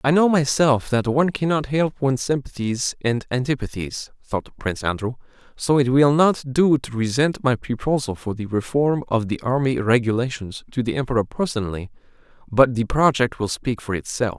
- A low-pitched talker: Yes, low, 125 Hz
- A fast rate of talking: No, average, 170 wpm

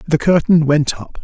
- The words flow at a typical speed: Yes, average, 195 wpm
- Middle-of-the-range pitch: Yes, medium, 155 Hz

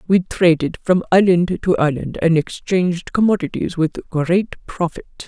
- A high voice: No, medium, 175 Hz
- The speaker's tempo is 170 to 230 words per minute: No, slow, 135 wpm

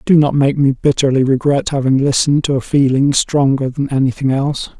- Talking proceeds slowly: No, average, 190 wpm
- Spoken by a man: Yes, male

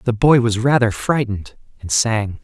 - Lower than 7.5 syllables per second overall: Yes, 4.7 syllables/s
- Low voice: Yes, low, 115 Hz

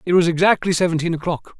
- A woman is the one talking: No, male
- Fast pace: No, average, 190 wpm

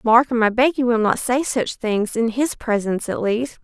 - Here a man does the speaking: No, female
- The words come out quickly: Yes, fast, 230 wpm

